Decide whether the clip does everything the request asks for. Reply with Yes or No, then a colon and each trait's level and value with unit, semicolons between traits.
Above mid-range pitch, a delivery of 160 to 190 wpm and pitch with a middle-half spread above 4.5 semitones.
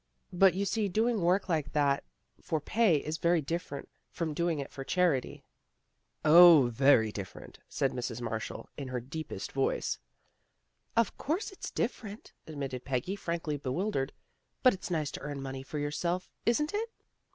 No: medium, 155 Hz; average, 170 wpm; wide, 5.4 semitones